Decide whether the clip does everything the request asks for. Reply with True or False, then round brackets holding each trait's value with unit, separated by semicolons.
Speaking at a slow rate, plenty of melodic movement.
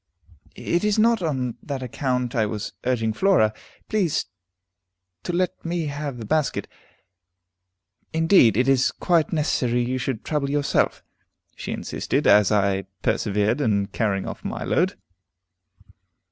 True (130 wpm; 6.2 semitones)